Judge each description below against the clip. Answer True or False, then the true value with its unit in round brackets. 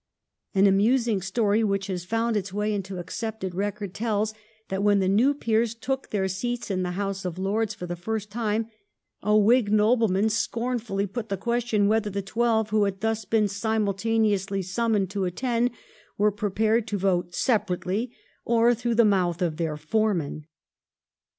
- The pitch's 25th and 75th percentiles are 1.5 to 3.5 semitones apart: True (2.7 semitones)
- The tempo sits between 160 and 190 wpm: True (165 wpm)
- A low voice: False (210 Hz)